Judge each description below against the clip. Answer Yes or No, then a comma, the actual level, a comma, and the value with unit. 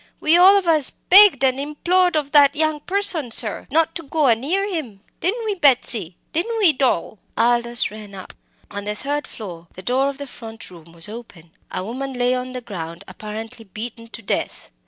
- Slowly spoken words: No, average, 200 wpm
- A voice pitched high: Yes, very high, 255 Hz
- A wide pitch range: Yes, wide, 6.3 semitones